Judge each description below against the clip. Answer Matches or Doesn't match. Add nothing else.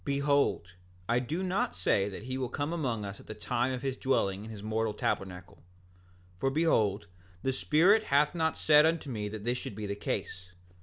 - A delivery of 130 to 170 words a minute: Doesn't match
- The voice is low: Matches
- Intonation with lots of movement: Matches